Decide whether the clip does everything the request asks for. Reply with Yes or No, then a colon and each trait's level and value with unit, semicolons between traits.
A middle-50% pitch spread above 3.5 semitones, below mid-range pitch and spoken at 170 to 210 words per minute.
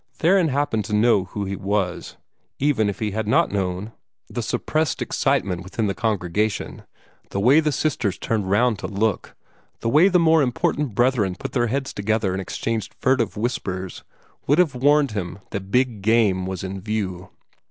Yes: average, 5.0 semitones; low, 110 Hz; average, 175 wpm